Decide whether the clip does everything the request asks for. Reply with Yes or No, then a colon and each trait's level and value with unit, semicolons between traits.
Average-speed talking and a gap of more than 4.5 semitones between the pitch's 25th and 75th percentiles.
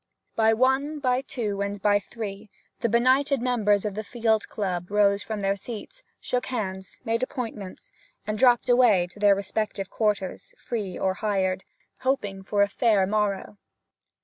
No: average, 155 wpm; average, 3.5 semitones